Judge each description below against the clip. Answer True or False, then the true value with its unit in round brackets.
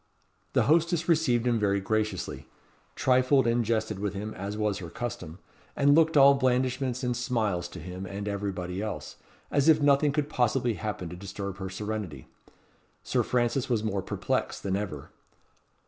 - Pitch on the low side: True (110 Hz)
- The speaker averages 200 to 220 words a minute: False (160 wpm)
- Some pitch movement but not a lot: True (4.8 semitones)